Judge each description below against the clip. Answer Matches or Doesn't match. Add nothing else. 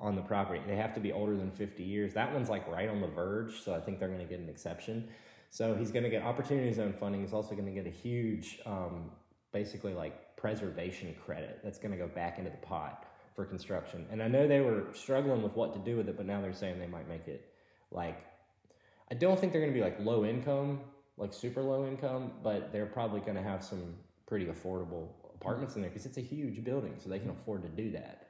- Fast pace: Matches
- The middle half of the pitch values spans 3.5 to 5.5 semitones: Matches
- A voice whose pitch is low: Matches